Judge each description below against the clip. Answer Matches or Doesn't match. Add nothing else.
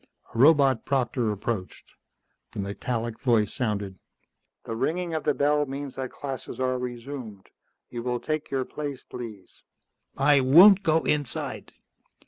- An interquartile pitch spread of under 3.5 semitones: Doesn't match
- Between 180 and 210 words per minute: Doesn't match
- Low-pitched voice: Matches